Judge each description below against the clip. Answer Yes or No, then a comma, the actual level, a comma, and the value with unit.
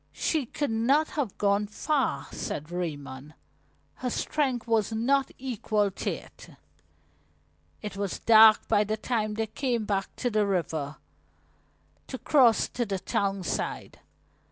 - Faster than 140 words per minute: No, slow, 135 wpm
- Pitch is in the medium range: No, high, 215 Hz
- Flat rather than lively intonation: No, average, 4.0 semitones